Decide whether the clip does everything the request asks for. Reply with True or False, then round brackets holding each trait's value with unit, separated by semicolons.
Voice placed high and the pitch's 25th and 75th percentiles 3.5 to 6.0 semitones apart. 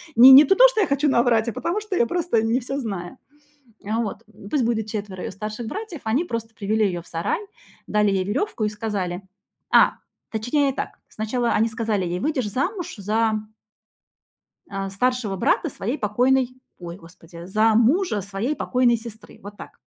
True (225 Hz; 4.3 semitones)